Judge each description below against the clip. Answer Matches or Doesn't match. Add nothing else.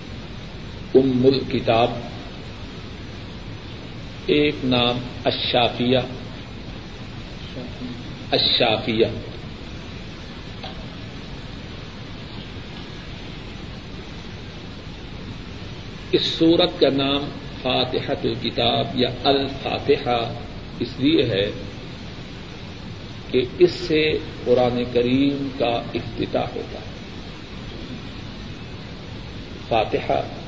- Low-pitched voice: Matches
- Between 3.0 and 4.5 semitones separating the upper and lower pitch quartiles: Doesn't match